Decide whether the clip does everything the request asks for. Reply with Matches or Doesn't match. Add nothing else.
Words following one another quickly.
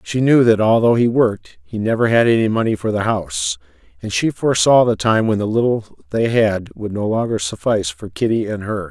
Matches